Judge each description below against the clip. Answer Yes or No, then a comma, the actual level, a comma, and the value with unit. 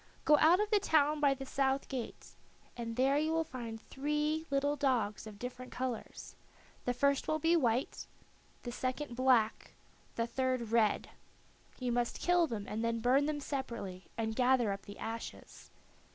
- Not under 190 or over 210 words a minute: No, average, 165 wpm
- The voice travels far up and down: No, average, 3.9 semitones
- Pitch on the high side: Yes, very high, 255 Hz